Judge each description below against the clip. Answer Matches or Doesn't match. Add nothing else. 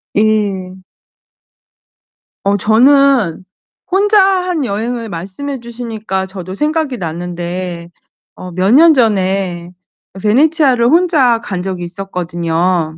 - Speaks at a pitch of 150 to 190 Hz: Doesn't match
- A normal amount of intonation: Doesn't match